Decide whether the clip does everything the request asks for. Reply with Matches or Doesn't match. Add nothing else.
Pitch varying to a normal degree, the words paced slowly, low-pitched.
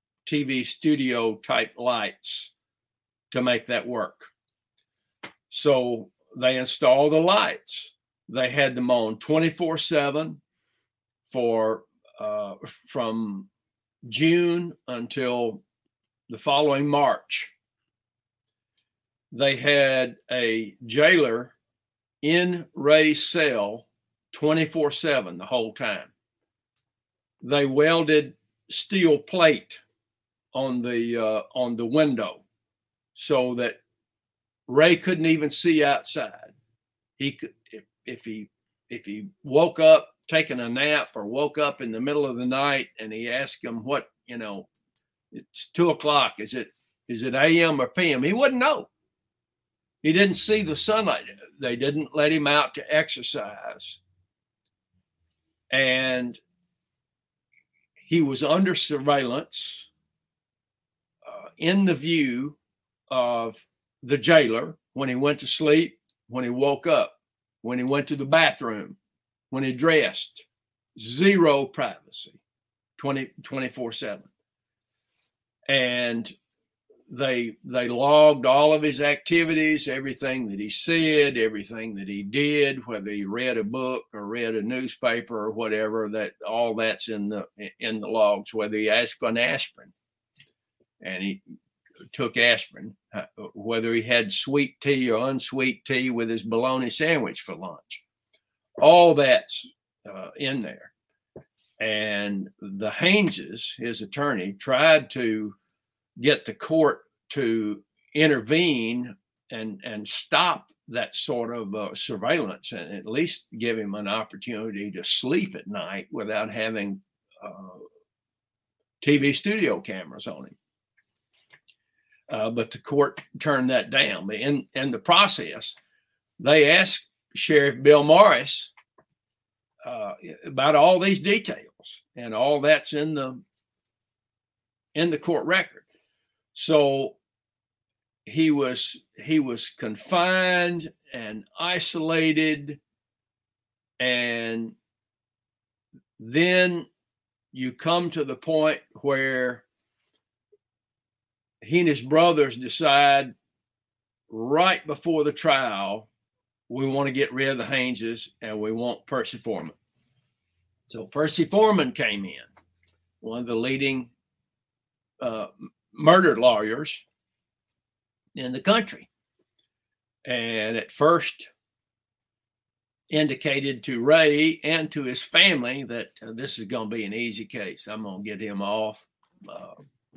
Matches